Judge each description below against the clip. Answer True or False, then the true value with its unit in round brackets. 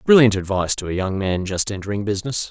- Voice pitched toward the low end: True (100 Hz)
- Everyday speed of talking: False (215 wpm)